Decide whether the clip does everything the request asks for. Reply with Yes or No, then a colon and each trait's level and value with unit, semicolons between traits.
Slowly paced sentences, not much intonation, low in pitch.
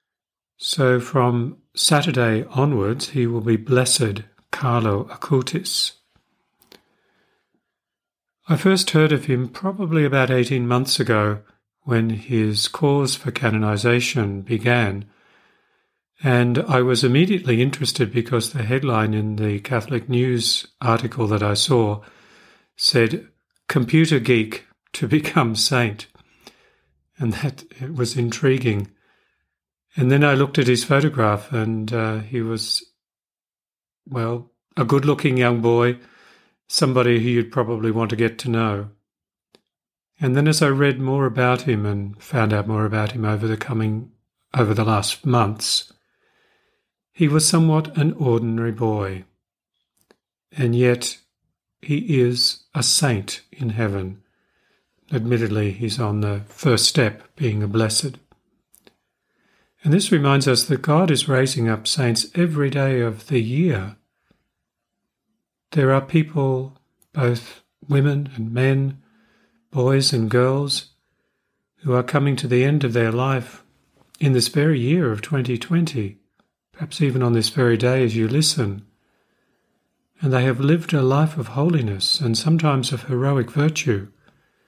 No: slow, 130 wpm; average, 3.9 semitones; low, 125 Hz